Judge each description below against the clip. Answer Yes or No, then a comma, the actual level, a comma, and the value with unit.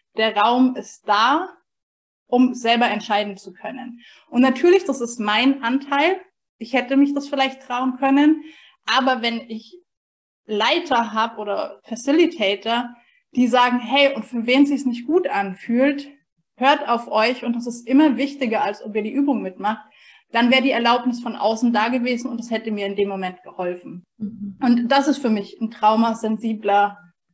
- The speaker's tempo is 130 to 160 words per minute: No, average, 170 wpm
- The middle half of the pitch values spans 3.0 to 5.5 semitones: Yes, average, 3.9 semitones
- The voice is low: No, high, 240 Hz